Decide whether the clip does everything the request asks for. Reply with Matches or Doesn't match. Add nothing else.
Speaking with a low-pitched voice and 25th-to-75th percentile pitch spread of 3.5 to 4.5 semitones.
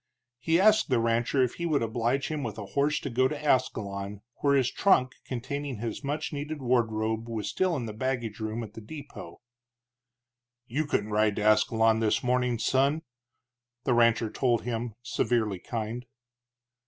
Matches